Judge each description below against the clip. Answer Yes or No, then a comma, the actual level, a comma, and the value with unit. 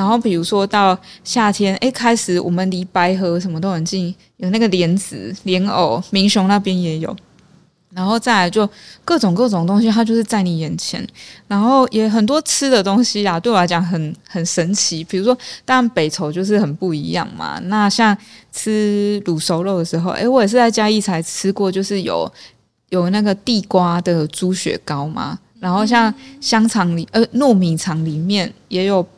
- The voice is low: No, high, 195 Hz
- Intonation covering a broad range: No, average, 3.7 semitones